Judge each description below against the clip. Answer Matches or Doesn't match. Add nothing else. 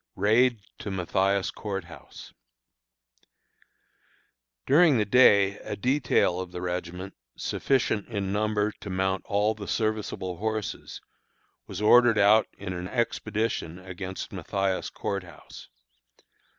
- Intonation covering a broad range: Doesn't match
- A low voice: Matches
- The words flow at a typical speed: Doesn't match